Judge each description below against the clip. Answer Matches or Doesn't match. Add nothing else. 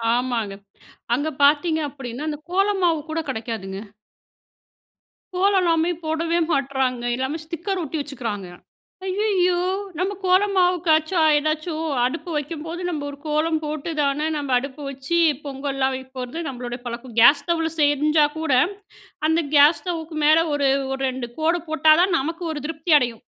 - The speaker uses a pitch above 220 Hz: Matches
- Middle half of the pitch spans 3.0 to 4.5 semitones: Matches